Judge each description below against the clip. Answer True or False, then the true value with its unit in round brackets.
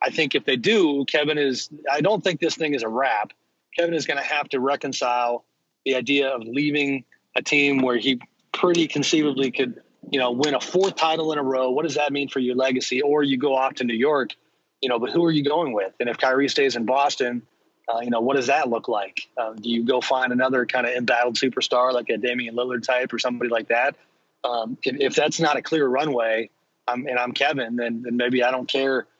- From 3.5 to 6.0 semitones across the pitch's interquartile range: False (2.9 semitones)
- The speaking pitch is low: True (130 Hz)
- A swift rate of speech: True (235 wpm)